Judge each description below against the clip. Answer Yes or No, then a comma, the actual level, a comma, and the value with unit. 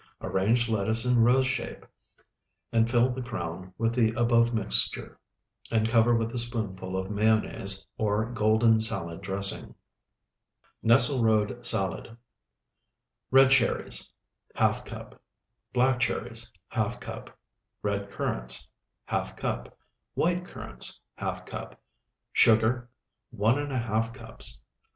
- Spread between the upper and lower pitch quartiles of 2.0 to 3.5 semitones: Yes, average, 2.7 semitones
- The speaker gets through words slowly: Yes, slow, 110 wpm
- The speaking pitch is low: Yes, low, 115 Hz